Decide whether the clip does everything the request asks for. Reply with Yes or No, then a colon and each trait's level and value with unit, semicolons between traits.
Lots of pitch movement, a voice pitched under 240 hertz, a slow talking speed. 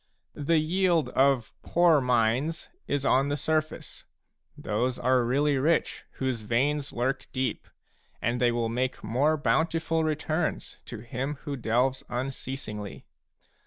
No: average, 4.0 semitones; low, 135 Hz; slow, 125 wpm